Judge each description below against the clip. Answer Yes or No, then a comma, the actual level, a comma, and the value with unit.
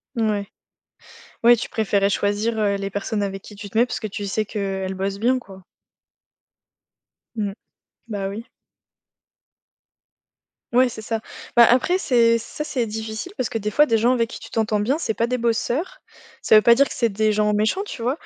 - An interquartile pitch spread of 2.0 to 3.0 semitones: Yes, average, 2.7 semitones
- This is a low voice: No, high, 220 Hz